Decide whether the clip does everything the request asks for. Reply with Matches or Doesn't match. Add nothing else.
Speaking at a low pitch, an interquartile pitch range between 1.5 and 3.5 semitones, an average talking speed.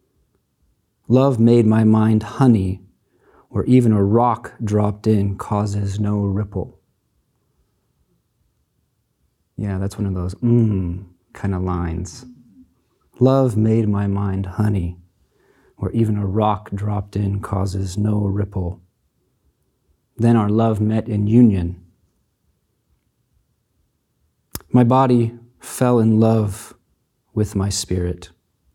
Doesn't match